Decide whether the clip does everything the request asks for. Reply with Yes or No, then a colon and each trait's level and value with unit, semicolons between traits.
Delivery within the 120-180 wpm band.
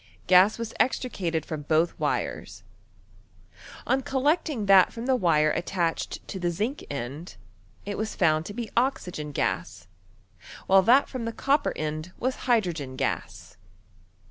Yes: average, 140 wpm